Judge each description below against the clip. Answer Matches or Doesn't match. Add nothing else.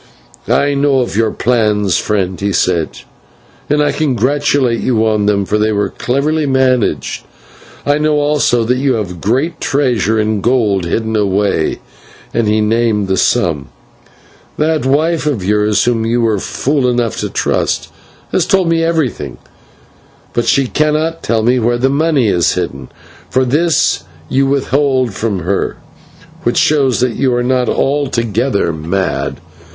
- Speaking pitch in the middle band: Doesn't match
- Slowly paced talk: Doesn't match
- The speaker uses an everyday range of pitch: Matches